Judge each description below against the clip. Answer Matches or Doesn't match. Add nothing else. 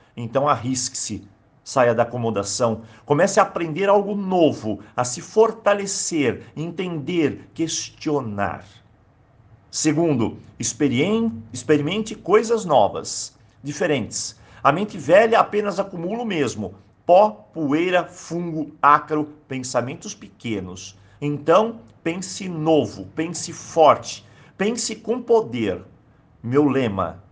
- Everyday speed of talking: Doesn't match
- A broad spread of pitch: Matches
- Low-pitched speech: Doesn't match